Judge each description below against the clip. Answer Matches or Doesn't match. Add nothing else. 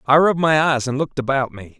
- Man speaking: Matches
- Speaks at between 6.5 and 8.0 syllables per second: Matches